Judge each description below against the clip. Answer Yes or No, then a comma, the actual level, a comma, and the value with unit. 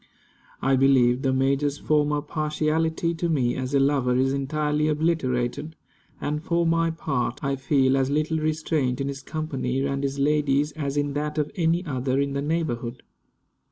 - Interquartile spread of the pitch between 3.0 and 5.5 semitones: No, narrow, 2.4 semitones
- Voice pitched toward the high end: No, medium, 145 Hz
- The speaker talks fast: No, average, 165 wpm